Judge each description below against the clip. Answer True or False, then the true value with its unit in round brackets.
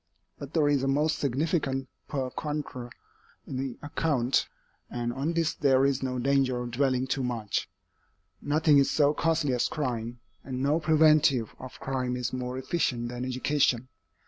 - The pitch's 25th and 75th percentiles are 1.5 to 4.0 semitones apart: True (2.8 semitones)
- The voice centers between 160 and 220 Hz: False (135 Hz)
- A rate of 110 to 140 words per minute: False (160 wpm)